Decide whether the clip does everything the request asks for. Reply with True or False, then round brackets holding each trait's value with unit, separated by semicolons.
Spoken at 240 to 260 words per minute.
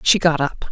True (250 wpm)